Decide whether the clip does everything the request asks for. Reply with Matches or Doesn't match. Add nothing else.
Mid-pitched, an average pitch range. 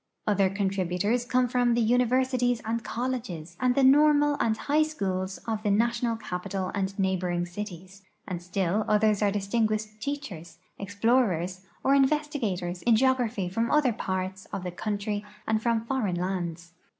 Doesn't match